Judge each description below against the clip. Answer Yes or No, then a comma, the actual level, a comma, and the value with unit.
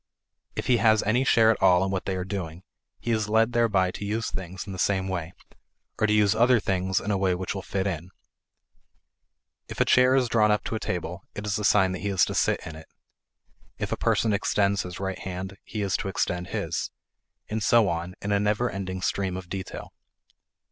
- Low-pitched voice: Yes, low, 100 Hz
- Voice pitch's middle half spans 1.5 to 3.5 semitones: Yes, narrow, 2.4 semitones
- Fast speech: Yes, fast, 225 wpm